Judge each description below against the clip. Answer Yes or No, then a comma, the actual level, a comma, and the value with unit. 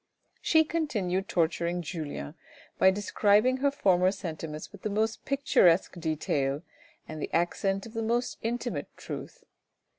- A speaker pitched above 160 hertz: Yes, high, 190 Hz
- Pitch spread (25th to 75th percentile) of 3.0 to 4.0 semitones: No, average, 5.3 semitones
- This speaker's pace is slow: Yes, slow, 130 wpm